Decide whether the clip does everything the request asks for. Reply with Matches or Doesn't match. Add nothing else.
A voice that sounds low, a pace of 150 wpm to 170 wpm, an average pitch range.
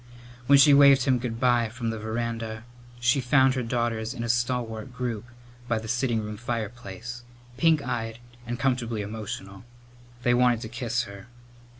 Doesn't match